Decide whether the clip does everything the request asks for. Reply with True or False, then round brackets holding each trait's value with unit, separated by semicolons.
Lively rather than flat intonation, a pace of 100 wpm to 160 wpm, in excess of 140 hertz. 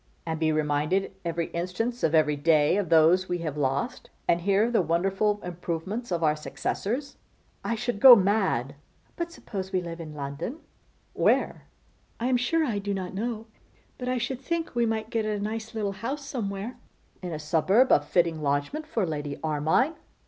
False (6.3 semitones; 180 wpm; 190 Hz)